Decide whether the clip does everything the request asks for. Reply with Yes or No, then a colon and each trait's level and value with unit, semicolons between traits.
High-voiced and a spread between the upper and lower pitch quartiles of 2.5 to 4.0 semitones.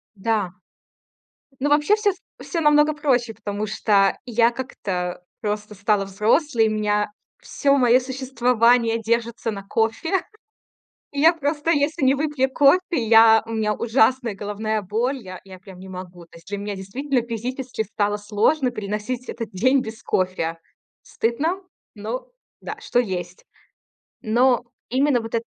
No: high, 230 Hz; average, 4.4 semitones